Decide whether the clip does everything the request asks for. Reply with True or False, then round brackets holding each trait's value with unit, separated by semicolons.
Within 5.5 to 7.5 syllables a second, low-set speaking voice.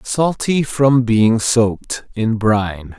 False (3.2 syllables/s; 115 Hz)